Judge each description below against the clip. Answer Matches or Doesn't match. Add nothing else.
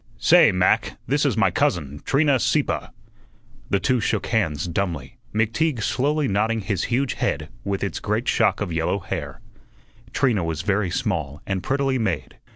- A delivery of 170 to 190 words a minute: Doesn't match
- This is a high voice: Doesn't match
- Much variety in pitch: Matches